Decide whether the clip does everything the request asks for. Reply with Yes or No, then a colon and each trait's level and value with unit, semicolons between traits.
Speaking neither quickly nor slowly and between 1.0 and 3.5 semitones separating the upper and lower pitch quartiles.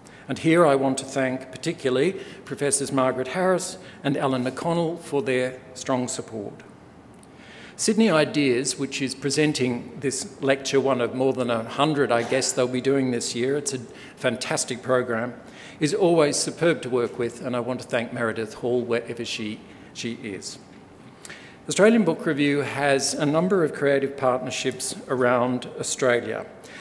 Yes: average, 150 wpm; narrow, 2.4 semitones